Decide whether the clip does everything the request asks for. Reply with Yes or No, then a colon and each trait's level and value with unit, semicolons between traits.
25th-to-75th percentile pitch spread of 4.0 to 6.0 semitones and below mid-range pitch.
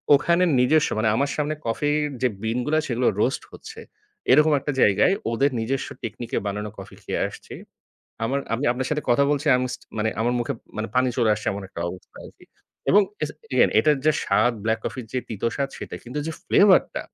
Yes: average, 4.7 semitones; low, 125 Hz